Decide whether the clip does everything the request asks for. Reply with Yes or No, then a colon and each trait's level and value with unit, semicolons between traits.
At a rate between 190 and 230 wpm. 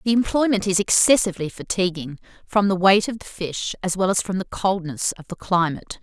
Yes: average, 200 wpm